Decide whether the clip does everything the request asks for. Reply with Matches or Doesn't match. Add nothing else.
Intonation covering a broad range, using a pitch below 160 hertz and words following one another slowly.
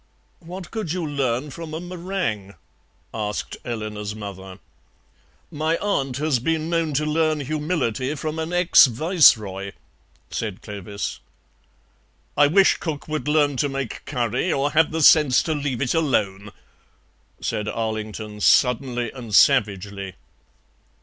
Matches